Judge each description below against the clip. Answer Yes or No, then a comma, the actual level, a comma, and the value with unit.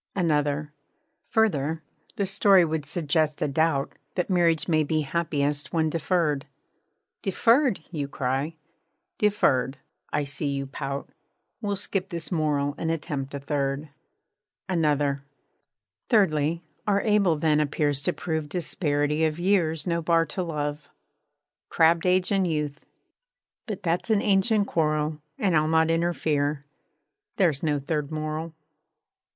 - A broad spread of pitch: No, average, 3.2 semitones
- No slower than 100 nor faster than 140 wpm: Yes, slow, 135 wpm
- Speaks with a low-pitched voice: No, medium, 155 Hz